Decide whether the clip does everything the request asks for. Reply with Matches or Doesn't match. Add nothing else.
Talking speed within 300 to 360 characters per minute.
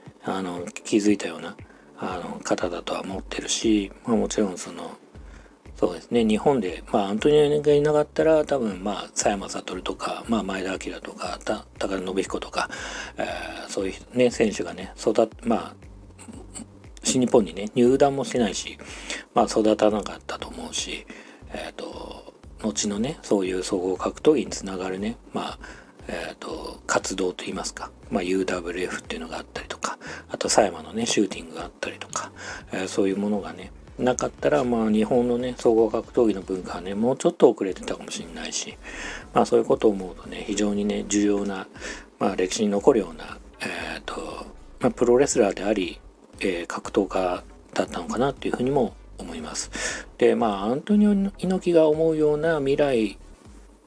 Matches